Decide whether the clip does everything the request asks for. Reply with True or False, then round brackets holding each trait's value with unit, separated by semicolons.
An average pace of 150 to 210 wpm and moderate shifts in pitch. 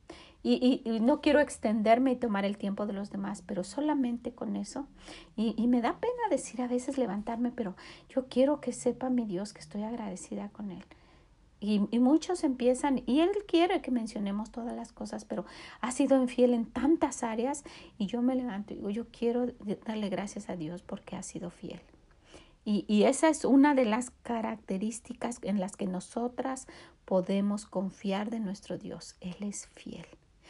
True (185 wpm; 4.1 semitones)